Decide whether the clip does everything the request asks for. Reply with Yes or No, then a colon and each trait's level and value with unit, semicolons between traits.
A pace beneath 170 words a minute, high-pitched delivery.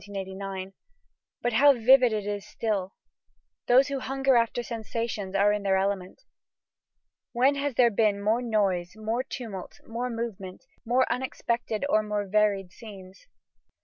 Yes: slow, 135 wpm; high, 220 Hz